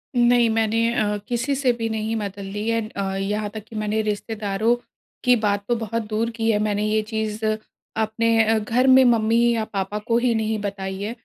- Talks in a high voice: Yes, high, 220 Hz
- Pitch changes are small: Yes, narrow, 1.6 semitones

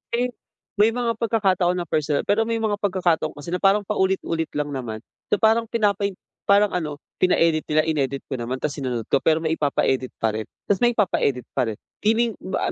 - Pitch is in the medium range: Yes, medium, 180 Hz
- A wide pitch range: Yes, wide, 6.3 semitones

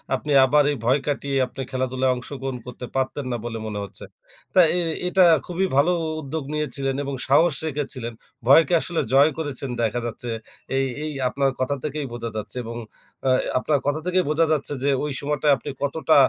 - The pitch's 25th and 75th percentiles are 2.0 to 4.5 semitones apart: Yes, average, 2.8 semitones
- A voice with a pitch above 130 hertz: Yes, medium, 140 Hz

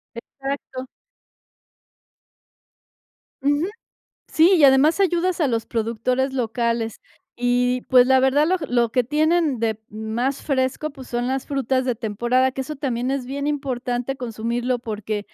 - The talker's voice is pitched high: Yes, very high, 255 Hz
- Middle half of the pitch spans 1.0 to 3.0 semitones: Yes, average, 2.7 semitones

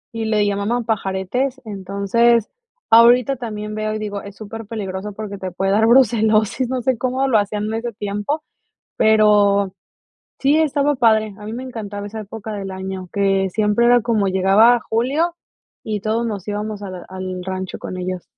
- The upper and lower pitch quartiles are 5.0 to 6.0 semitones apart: No, average, 2.8 semitones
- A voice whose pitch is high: Yes, high, 215 Hz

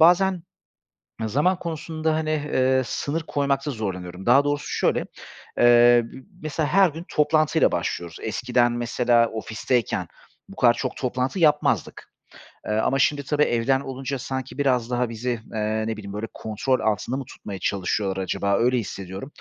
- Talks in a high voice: No, low, 125 Hz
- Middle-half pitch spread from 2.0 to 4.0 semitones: No, average, 4.8 semitones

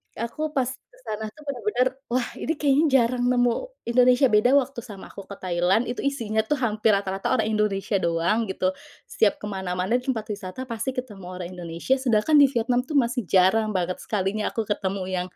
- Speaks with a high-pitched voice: Yes, high, 220 Hz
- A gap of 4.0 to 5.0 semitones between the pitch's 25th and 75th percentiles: Yes, average, 4.7 semitones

